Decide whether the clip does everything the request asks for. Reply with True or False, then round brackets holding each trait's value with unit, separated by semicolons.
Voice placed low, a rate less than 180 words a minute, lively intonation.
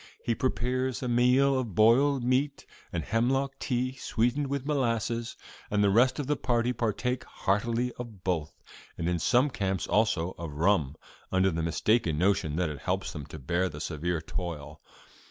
True (115 Hz; 170 wpm; 6.4 semitones)